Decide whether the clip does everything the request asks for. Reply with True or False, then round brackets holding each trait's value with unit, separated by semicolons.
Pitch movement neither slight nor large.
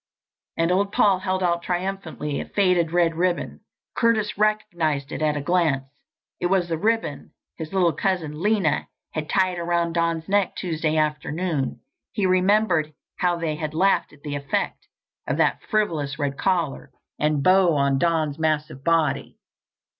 True (3.5 semitones)